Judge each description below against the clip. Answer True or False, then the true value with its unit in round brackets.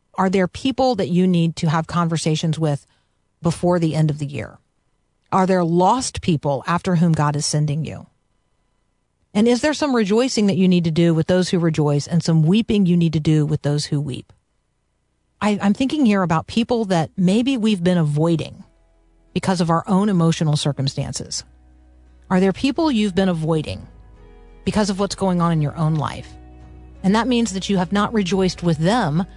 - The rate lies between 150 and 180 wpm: False (190 wpm)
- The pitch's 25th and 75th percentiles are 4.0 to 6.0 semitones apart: True (4.5 semitones)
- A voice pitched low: False (170 Hz)